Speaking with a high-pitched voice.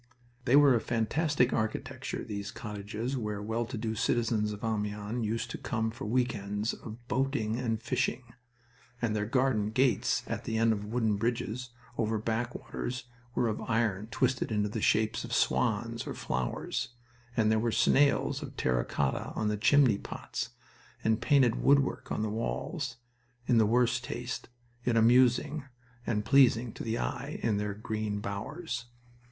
No: low, 115 Hz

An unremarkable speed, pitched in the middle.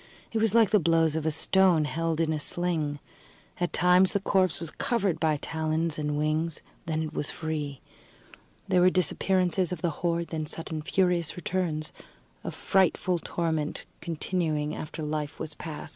Yes: average, 165 wpm; medium, 165 Hz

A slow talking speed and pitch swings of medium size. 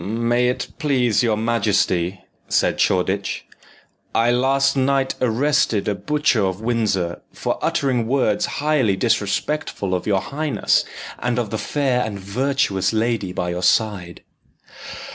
Yes: slow, 130 wpm; average, 4.9 semitones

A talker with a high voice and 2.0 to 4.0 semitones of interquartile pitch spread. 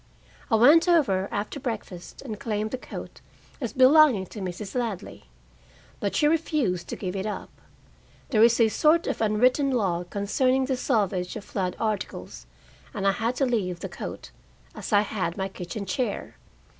No: high, 215 Hz; average, 4.8 semitones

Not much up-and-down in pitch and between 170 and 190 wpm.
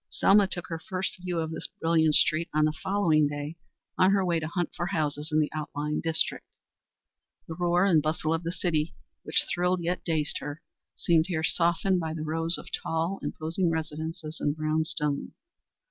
Yes: narrow, 2.1 semitones; average, 185 wpm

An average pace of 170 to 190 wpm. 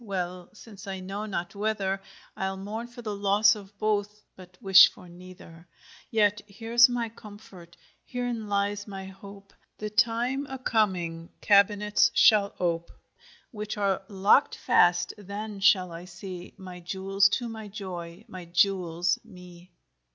No: average, 145 wpm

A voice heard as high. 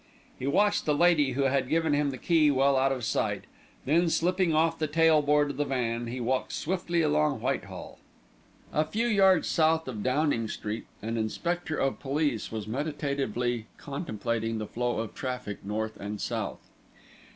No: medium, 140 Hz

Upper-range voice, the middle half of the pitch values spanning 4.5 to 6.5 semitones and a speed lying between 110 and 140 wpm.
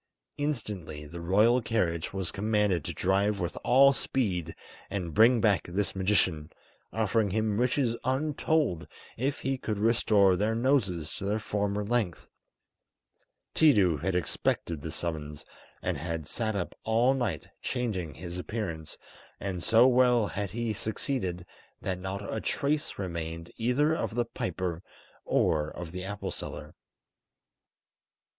No: low, 100 Hz; average, 5.1 semitones; slow, 135 wpm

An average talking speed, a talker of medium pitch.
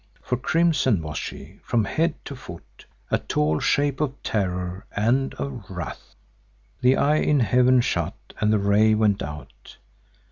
No: average, 150 wpm; low, 110 Hz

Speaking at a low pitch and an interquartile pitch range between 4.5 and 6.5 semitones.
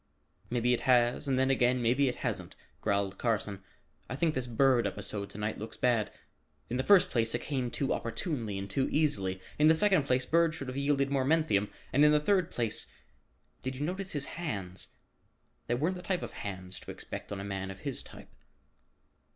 Yes: low, 125 Hz; wide, 5.6 semitones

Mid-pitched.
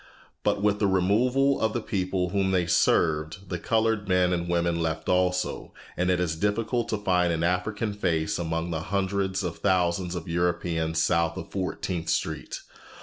No: very low, 90 Hz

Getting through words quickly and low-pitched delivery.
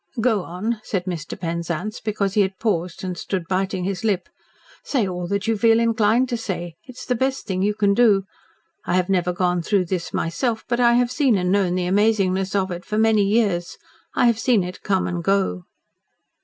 No: fast, 210 wpm; high, 195 Hz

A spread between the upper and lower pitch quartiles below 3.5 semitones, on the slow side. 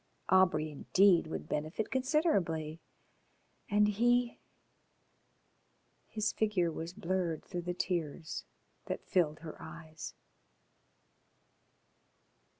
No: average, 4.7 semitones; slow, 85 wpm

